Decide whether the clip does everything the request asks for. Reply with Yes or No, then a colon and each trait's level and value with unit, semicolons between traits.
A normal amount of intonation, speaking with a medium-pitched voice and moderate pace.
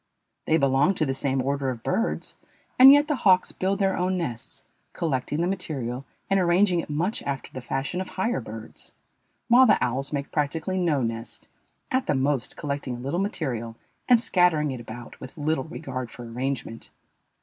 No: wide, 6.0 semitones; medium, 145 Hz; average, 180 wpm